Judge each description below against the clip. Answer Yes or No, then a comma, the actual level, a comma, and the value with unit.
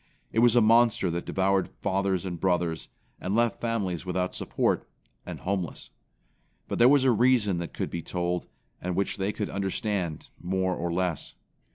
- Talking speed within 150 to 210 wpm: Yes, average, 170 wpm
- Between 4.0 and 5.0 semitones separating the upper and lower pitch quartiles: No, average, 3.5 semitones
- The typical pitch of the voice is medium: No, very low, 95 Hz